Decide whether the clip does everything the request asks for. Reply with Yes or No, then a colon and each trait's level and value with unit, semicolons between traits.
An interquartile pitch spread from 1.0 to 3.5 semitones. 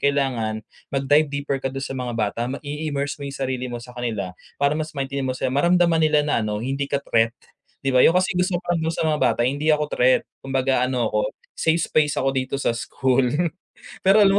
Yes: average, 3.1 semitones